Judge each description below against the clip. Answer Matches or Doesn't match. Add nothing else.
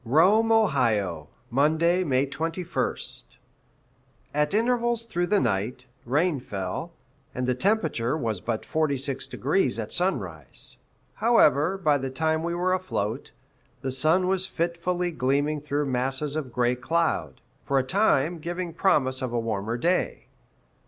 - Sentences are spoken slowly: Matches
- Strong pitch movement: Matches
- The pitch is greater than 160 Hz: Doesn't match